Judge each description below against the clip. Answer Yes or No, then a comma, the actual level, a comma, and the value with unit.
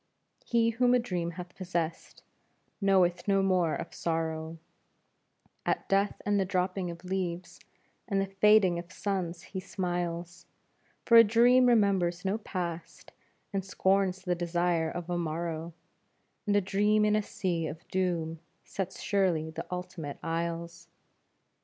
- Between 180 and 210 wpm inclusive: No, average, 140 wpm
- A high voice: No, medium, 180 Hz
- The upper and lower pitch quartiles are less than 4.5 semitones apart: Yes, narrow, 2.6 semitones